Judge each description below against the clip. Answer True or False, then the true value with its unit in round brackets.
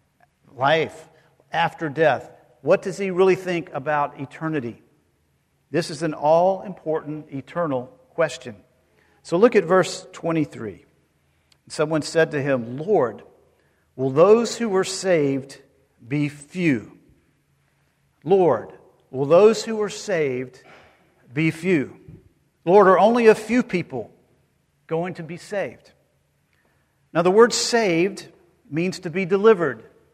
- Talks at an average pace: False (120 wpm)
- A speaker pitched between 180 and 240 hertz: False (165 Hz)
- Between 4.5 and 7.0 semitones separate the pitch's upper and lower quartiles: True (5.3 semitones)